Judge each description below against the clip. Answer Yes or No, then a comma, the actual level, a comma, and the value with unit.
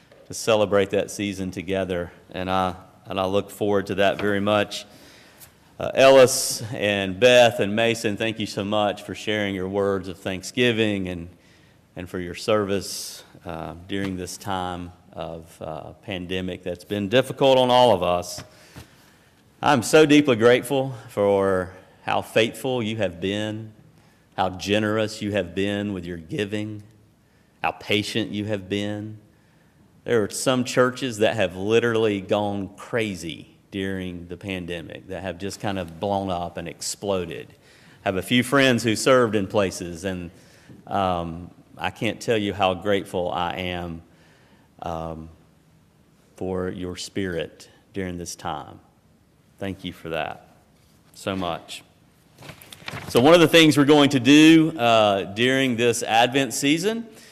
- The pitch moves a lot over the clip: No, average, 3.7 semitones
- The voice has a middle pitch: No, low, 100 Hz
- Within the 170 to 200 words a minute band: No, average, 145 wpm